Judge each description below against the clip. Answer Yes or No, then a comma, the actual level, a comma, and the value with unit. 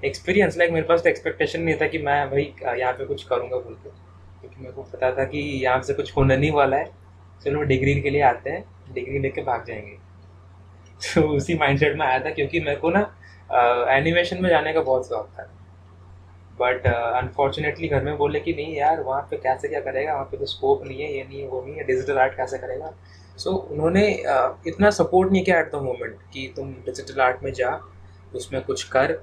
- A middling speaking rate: No, fast, 220 wpm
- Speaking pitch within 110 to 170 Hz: Yes, medium, 140 Hz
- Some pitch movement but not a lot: No, wide, 7.2 semitones